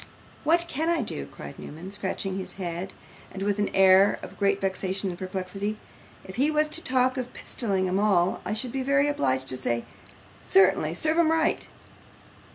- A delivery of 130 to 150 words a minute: No, average, 170 wpm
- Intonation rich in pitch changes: Yes, wide, 6.3 semitones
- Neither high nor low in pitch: No, high, 200 Hz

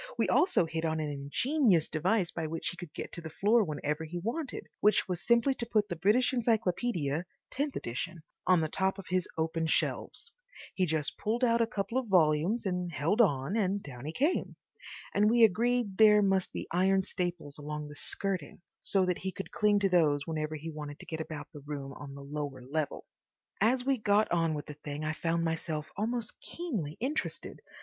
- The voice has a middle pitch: Yes, medium, 175 Hz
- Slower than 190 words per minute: No, average, 200 wpm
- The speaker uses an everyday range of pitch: No, wide, 5.7 semitones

